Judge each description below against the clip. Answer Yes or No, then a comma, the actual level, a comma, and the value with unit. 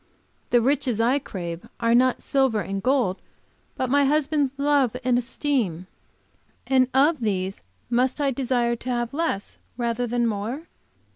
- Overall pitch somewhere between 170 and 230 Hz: No, high, 245 Hz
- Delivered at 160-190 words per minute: No, average, 145 wpm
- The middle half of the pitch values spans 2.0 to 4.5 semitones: Yes, average, 3.1 semitones